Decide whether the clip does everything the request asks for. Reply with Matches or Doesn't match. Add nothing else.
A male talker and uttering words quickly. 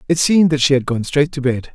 Matches